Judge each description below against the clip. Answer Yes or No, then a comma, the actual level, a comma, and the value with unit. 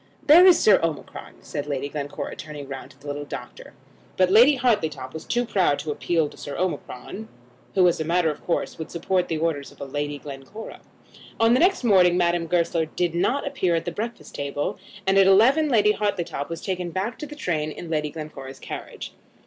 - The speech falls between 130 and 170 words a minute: No, average, 200 wpm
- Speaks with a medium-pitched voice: Yes, medium, 170 Hz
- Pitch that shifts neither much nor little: No, wide, 5.9 semitones